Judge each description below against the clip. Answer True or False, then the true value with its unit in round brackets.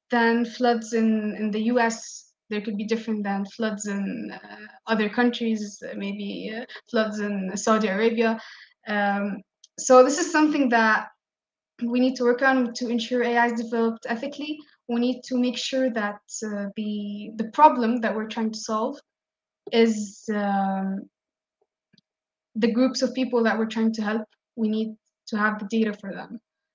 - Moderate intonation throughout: False (2.3 semitones)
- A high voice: True (225 Hz)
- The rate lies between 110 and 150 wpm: False (165 wpm)